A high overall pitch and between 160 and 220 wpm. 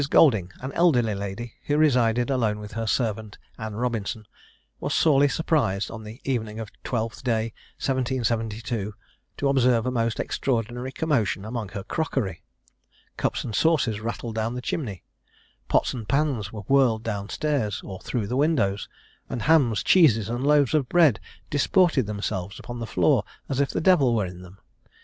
No: low, 115 Hz; average, 165 wpm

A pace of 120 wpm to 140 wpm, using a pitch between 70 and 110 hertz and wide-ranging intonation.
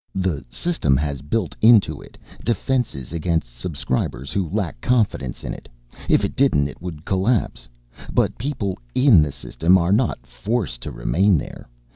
No: average, 155 wpm; very low, 90 Hz; wide, 7.5 semitones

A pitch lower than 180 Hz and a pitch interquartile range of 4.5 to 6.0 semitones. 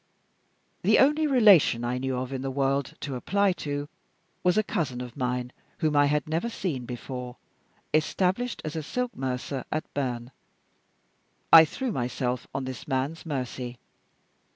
Yes: medium, 140 Hz; average, 4.8 semitones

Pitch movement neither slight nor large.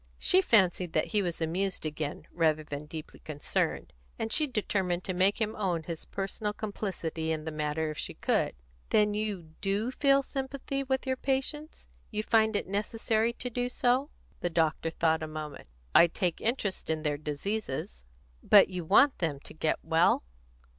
No: wide, 5.8 semitones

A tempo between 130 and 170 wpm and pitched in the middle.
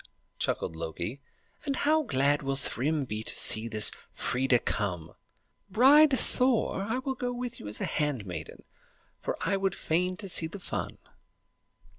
Yes: average, 150 wpm; medium, 155 Hz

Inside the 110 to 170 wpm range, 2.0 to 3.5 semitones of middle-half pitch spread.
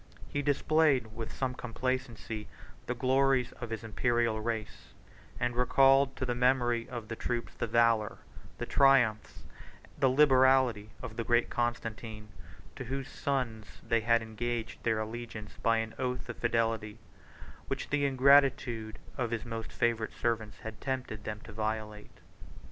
Yes: average, 145 wpm; narrow, 2.5 semitones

